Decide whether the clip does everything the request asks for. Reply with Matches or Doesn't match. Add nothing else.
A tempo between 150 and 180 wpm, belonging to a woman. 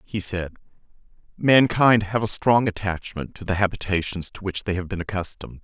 Doesn't match